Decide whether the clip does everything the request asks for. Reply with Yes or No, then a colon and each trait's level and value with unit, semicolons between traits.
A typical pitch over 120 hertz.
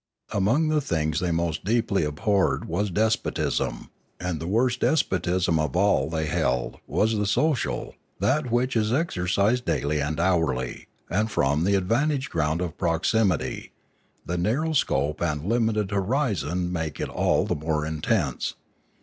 No: very low, 90 Hz